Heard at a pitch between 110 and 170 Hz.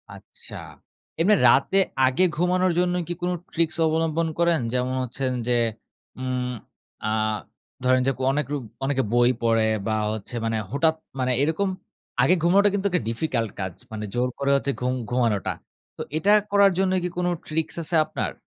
Yes: medium, 140 Hz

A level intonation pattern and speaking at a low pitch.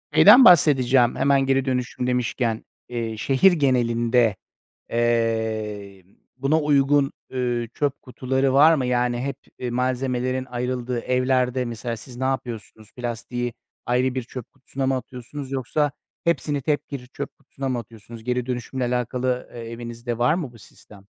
Yes: narrow, 2.1 semitones; low, 125 Hz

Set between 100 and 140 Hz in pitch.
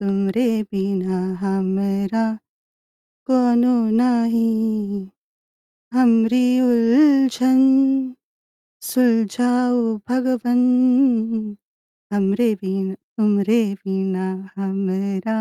No: high, 225 Hz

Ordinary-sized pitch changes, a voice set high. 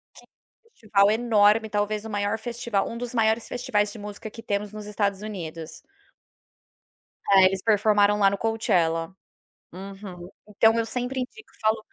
No: narrow, 2.0 semitones; high, 210 Hz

